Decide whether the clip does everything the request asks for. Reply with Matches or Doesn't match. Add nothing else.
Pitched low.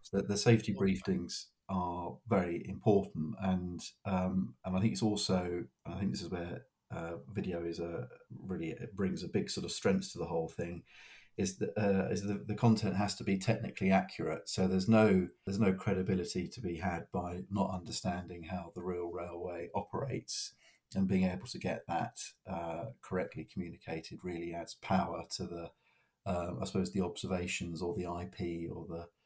Matches